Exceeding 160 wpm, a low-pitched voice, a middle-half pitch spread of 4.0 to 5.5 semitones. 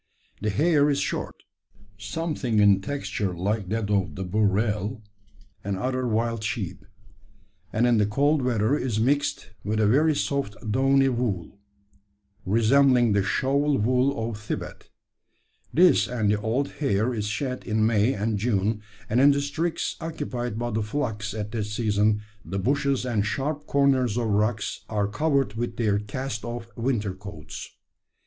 No: average, 150 wpm; low, 115 Hz; average, 4.4 semitones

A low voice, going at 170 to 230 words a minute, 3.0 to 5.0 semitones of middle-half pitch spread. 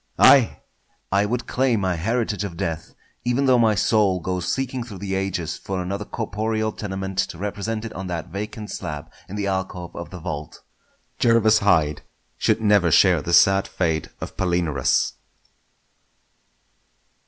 No: very low, 95 Hz; average, 155 wpm; average, 3.8 semitones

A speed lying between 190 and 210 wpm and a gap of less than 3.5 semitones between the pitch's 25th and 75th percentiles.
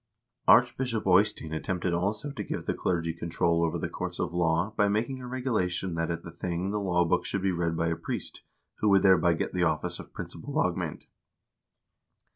No: average, 195 wpm; average, 3.8 semitones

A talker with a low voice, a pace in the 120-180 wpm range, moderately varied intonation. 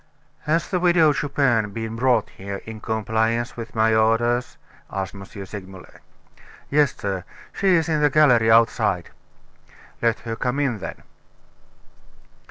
Yes: low, 115 Hz; slow, 135 wpm; average, 4.5 semitones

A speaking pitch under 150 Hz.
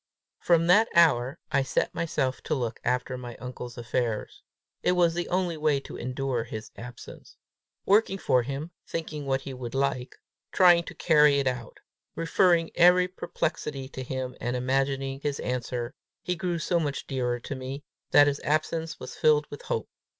Yes: medium, 140 Hz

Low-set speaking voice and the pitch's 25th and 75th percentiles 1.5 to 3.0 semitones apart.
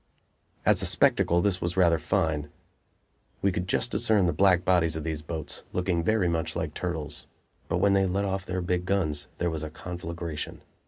Yes: very low, 90 Hz; narrow, 2.6 semitones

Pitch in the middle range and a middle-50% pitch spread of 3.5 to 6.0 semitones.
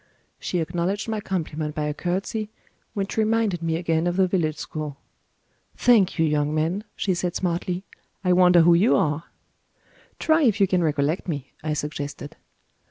Yes: medium, 175 Hz; average, 3.8 semitones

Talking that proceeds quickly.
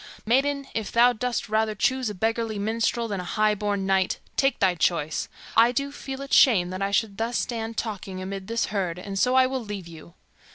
Yes: fast, 210 wpm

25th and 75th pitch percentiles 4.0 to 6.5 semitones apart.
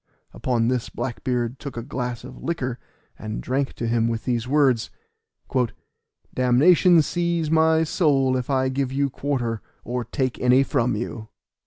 No: average, 2.9 semitones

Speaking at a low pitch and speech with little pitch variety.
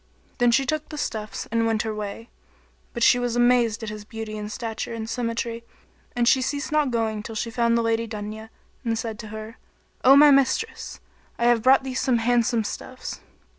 No: high, 230 Hz; narrow, 1.9 semitones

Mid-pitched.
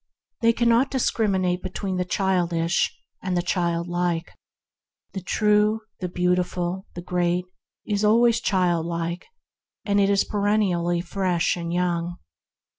Yes: medium, 180 Hz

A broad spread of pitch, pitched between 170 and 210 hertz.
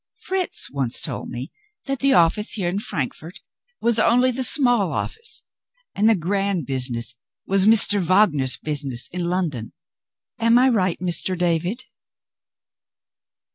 Yes: wide, 6.7 semitones; medium, 185 Hz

